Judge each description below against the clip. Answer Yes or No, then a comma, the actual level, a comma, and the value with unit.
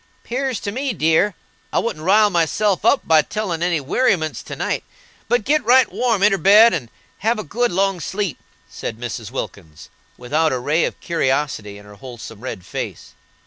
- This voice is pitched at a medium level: Yes, medium, 170 Hz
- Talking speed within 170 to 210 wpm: Yes, average, 180 wpm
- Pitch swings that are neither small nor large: No, wide, 8.5 semitones